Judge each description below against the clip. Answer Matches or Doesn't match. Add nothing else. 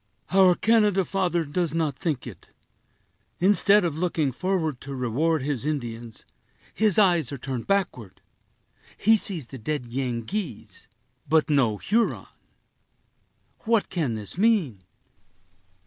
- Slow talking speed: Matches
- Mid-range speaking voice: Matches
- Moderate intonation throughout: Doesn't match